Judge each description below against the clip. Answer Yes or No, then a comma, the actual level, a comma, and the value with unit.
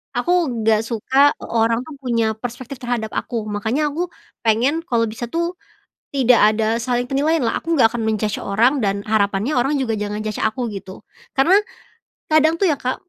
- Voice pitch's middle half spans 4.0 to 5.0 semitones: Yes, average, 4.4 semitones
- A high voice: Yes, high, 240 Hz